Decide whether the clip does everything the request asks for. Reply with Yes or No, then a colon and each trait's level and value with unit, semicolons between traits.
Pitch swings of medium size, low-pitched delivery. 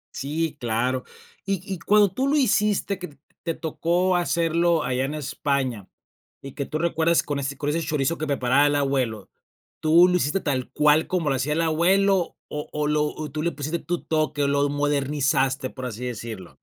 No: average, 3.7 semitones; medium, 150 Hz